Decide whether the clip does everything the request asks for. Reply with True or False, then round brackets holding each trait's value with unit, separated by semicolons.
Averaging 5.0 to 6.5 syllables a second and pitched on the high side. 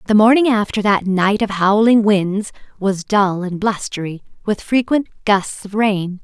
False (4.1 syllables/s; 205 Hz)